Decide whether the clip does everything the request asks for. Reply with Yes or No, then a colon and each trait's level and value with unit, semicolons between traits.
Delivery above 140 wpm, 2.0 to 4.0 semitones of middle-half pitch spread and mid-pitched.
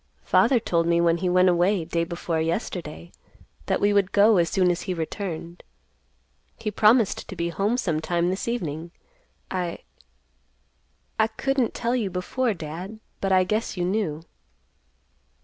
Yes: average, 150 wpm; average, 3.7 semitones; medium, 180 Hz